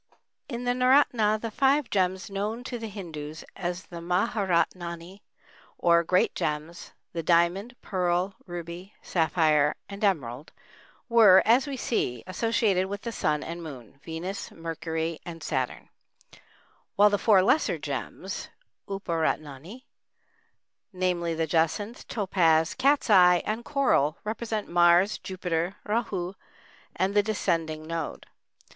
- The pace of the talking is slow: Yes, slow, 115 wpm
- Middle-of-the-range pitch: Yes, medium, 180 Hz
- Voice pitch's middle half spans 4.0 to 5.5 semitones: Yes, average, 4.3 semitones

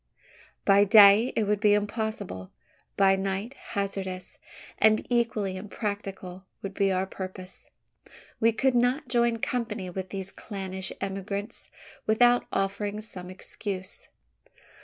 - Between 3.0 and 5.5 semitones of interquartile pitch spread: No, narrow, 2.4 semitones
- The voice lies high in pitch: Yes, high, 200 Hz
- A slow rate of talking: Yes, slow, 115 wpm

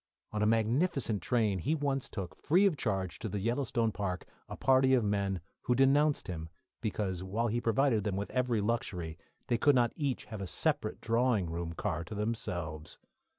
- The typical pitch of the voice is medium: No, low, 110 Hz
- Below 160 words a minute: No, average, 185 wpm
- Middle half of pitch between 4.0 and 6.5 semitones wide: Yes, average, 5.1 semitones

